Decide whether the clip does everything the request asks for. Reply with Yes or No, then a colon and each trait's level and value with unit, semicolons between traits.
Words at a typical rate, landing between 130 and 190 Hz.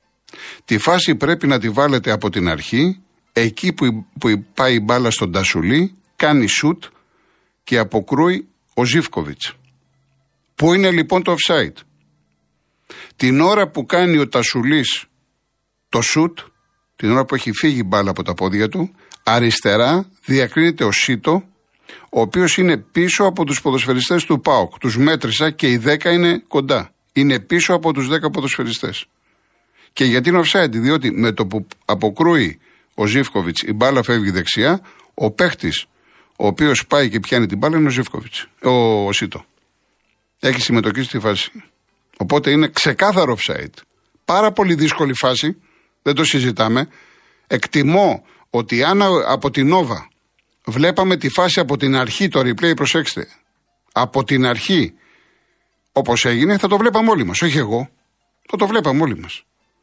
Yes: average, 150 wpm; low, 135 Hz